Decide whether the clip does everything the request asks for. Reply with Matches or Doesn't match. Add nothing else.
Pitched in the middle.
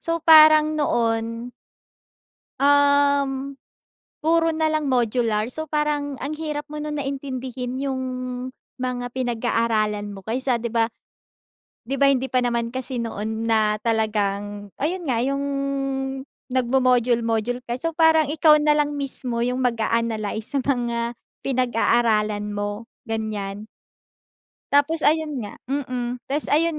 Doesn't match